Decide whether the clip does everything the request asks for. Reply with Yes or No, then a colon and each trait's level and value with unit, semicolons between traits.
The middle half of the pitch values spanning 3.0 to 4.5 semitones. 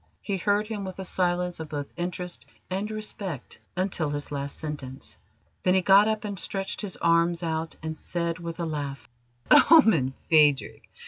Yes: average, 3.7 semitones